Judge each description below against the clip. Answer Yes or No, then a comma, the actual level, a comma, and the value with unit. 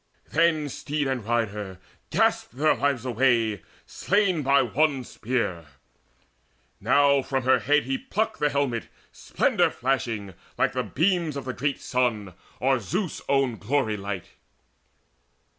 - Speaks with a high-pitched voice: No, low, 130 Hz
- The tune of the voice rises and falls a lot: No, average, 4.1 semitones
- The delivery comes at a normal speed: No, slow, 130 wpm